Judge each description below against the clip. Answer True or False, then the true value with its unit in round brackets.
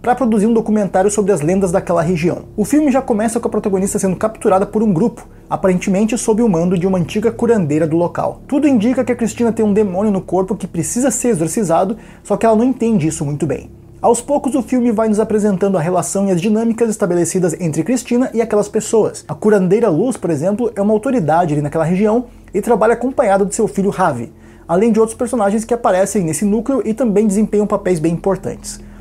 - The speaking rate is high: True (215 wpm)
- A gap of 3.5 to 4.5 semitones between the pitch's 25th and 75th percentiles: True (3.9 semitones)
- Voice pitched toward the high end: True (210 Hz)